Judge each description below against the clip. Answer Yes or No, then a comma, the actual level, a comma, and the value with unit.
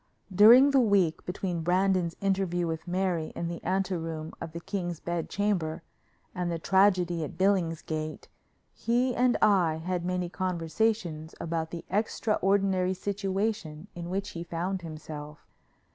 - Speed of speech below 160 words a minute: Yes, average, 140 wpm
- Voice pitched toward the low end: No, medium, 180 Hz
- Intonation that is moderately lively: Yes, average, 3.0 semitones